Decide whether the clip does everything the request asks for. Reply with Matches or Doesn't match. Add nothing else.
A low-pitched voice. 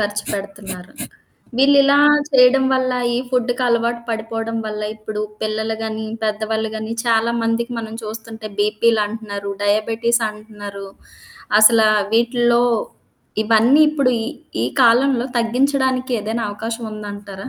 Doesn't match